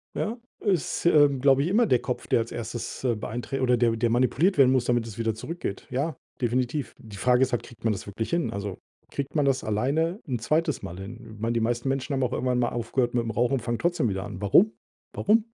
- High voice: No, low, 125 Hz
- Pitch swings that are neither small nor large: Yes, average, 3.5 semitones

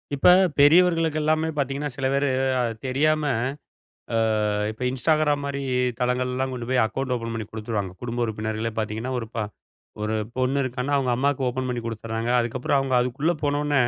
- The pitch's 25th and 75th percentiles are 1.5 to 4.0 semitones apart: Yes, average, 3.5 semitones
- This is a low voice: Yes, low, 130 Hz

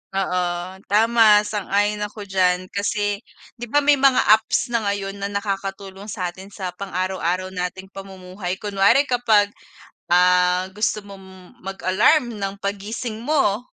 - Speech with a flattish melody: Yes, narrow, 2.1 semitones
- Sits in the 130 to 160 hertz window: No, high, 200 Hz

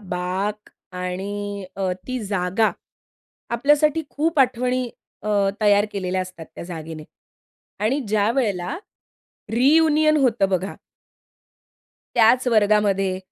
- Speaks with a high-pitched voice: Yes, high, 205 Hz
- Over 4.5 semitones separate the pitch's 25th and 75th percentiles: Yes, average, 5.1 semitones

